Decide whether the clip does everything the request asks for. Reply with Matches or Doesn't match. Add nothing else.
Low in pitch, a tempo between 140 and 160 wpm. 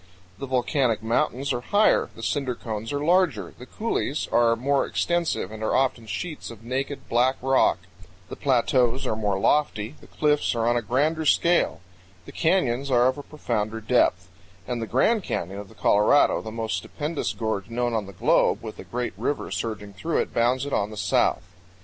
Doesn't match